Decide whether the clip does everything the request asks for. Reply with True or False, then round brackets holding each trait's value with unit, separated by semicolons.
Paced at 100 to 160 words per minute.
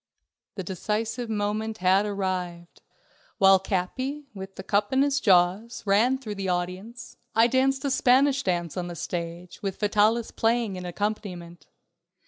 True (145 wpm)